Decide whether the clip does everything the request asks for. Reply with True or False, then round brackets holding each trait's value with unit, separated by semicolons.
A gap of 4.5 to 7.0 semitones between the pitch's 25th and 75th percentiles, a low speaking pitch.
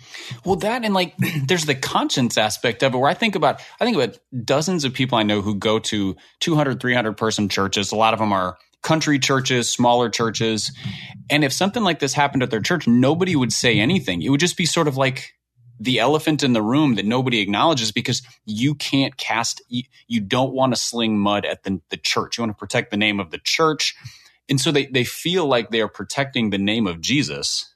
True (4.9 semitones; 130 Hz)